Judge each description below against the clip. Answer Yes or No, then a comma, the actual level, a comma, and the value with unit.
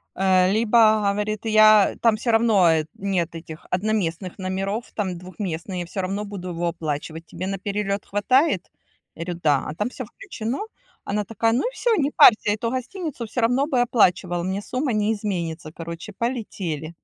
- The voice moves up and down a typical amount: Yes, average, 4.2 semitones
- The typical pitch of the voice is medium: No, high, 200 Hz